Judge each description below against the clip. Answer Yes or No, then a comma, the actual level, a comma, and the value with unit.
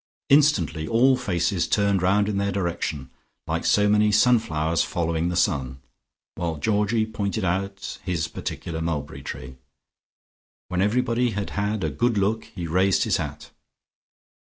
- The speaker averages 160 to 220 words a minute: No, average, 140 wpm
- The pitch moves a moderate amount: Yes, average, 4.2 semitones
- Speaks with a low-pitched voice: Yes, low, 100 Hz